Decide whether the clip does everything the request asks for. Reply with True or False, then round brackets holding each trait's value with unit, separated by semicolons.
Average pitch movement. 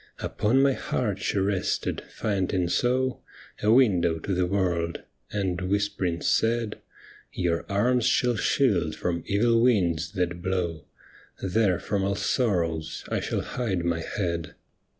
True (4.3 semitones)